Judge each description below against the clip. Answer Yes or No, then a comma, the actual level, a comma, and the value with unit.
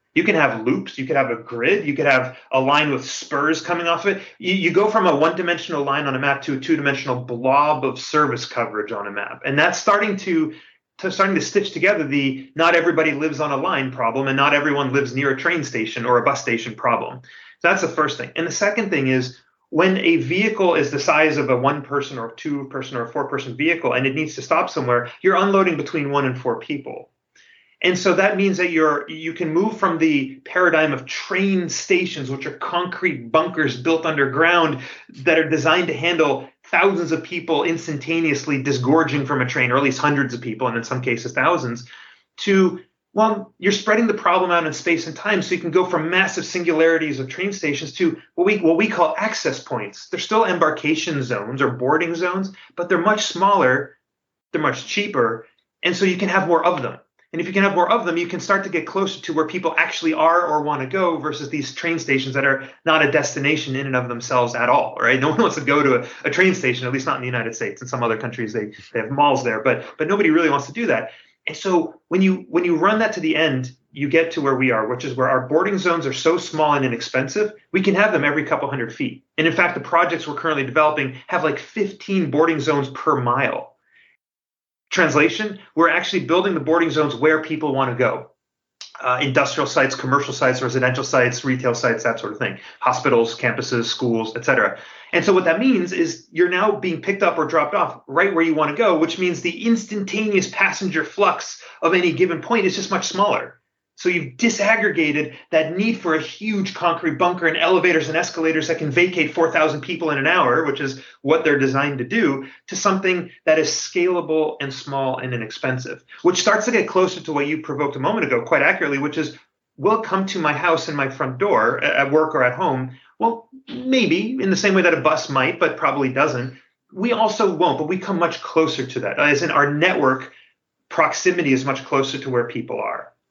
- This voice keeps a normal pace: No, fast, 225 wpm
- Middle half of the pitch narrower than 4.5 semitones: No, average, 4.8 semitones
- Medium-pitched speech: Yes, medium, 160 Hz